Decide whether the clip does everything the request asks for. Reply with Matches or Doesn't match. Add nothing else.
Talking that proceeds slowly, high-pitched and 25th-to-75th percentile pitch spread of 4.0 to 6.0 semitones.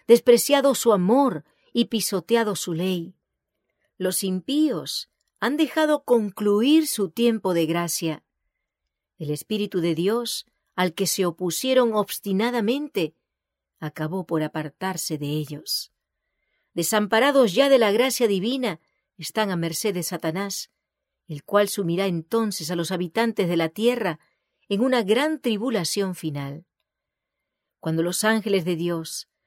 Matches